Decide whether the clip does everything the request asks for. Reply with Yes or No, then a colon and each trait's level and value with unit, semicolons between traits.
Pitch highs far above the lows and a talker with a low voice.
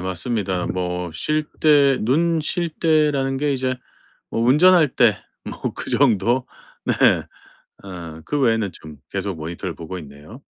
Yes: wide, 8.6 semitones; low, 115 Hz